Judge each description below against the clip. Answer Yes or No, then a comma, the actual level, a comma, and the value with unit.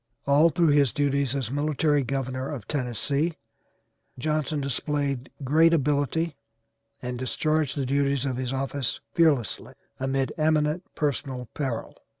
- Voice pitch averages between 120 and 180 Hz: Yes, medium, 140 Hz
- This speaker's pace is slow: Yes, slow, 125 wpm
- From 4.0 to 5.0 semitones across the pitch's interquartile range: No, narrow, 2.6 semitones